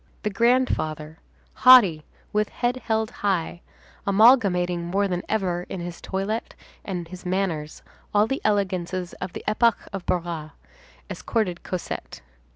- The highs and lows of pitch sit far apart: No, average, 3.7 semitones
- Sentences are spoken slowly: Yes, slow, 130 wpm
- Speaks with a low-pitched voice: No, high, 190 Hz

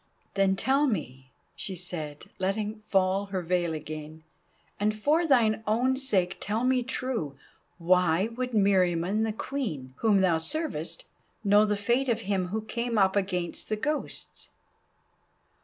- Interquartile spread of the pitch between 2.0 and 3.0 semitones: No, average, 4.6 semitones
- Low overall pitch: No, high, 200 Hz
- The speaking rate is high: No, average, 140 wpm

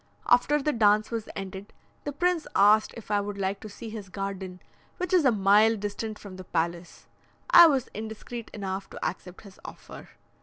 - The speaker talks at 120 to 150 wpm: No, average, 185 wpm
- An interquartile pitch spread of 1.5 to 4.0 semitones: Yes, average, 2.9 semitones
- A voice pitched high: Yes, high, 210 Hz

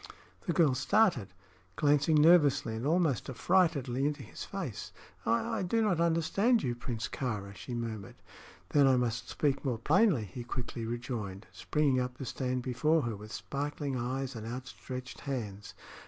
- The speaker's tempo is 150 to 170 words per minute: Yes, average, 155 wpm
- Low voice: Yes, low, 130 Hz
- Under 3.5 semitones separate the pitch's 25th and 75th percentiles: No, average, 4.4 semitones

